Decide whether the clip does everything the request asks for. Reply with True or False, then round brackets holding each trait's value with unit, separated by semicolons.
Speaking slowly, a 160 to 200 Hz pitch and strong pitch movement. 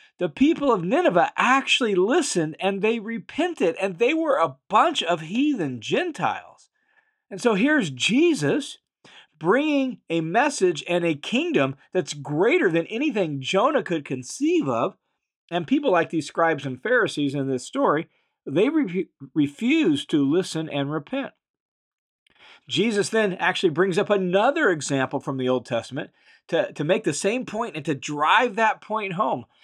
False (150 wpm; 190 Hz; 8.7 semitones)